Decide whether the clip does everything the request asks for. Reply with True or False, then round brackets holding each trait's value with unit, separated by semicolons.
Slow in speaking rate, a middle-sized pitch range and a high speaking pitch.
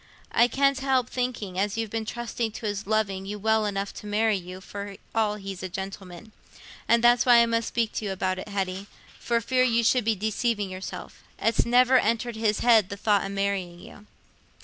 False (205 wpm; 3.0 semitones; 215 Hz)